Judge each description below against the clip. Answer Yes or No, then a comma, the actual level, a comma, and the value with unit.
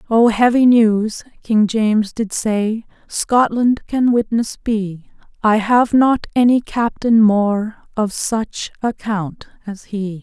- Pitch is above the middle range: Yes, high, 220 Hz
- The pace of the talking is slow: Yes, slow, 130 wpm